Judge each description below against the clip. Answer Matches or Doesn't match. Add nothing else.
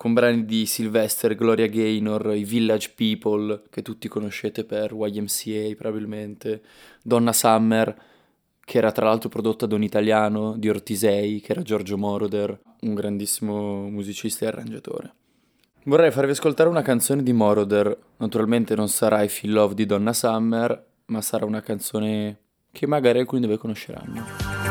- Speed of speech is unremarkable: Matches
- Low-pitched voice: Matches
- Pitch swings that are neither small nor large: Doesn't match